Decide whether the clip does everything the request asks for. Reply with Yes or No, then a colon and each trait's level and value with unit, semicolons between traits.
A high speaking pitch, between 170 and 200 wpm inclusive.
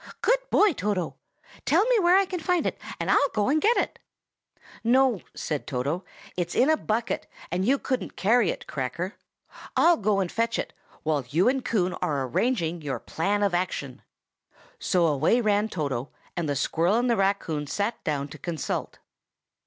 Yes: high, 195 Hz; average, 175 wpm